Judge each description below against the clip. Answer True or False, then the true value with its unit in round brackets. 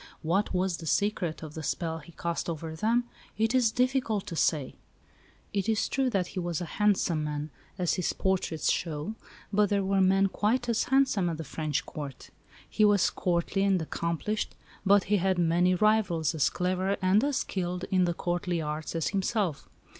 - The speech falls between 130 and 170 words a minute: False (180 wpm)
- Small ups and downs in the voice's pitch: False (3.9 semitones)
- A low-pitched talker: False (185 Hz)